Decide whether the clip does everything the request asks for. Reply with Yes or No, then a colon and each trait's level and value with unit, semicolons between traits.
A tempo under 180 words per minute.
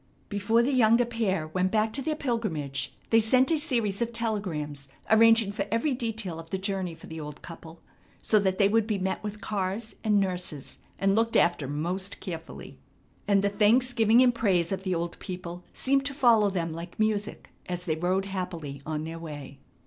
No: average, 190 wpm